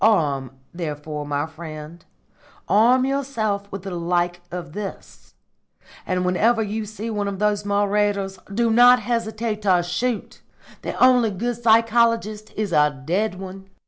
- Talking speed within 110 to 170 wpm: Yes, average, 140 wpm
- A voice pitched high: Yes, high, 205 Hz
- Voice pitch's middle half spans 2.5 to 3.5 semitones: No, average, 4.1 semitones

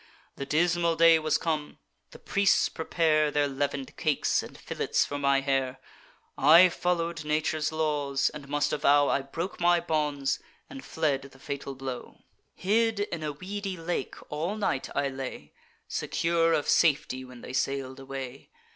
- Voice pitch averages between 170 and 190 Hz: No, medium, 150 Hz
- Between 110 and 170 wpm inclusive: Yes, average, 155 wpm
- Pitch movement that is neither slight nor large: Yes, average, 3.4 semitones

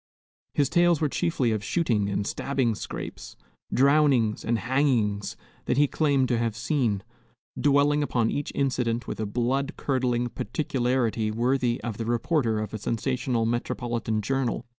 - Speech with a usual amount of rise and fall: Yes, average, 3.5 semitones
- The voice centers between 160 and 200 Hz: No, low, 120 Hz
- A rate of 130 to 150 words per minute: Yes, average, 145 wpm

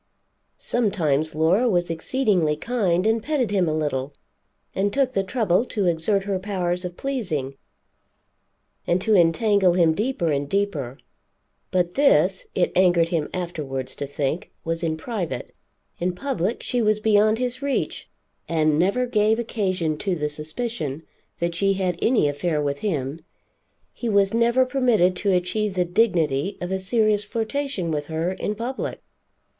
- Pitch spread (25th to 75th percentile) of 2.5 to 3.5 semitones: No, average, 5.2 semitones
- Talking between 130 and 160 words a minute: Yes, average, 150 wpm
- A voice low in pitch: No, medium, 185 Hz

